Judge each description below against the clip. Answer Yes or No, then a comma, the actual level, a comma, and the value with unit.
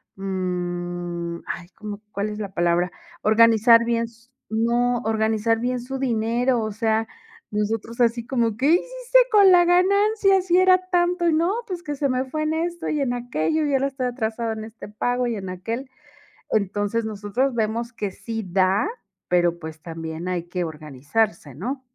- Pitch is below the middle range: No, high, 230 Hz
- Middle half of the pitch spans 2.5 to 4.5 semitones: No, wide, 5.5 semitones